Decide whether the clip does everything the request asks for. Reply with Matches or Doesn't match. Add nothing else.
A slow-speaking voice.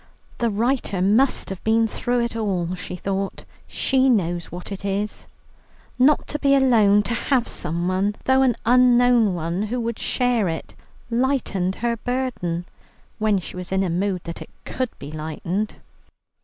Doesn't match